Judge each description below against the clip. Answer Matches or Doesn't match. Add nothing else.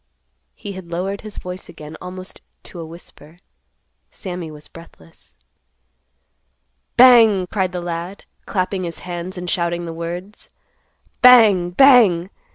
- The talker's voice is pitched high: Doesn't match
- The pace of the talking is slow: Matches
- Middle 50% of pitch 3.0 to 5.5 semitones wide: Doesn't match